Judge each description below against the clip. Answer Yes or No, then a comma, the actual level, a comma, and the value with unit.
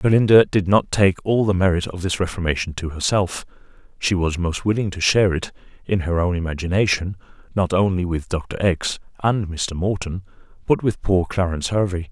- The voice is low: Yes, very low, 90 Hz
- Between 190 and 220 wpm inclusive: No, average, 175 wpm